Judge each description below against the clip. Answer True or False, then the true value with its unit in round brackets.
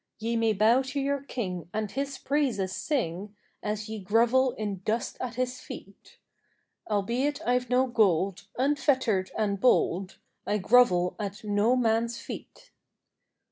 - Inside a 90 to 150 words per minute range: True (140 wpm)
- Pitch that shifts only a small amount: False (4.0 semitones)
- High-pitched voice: True (225 Hz)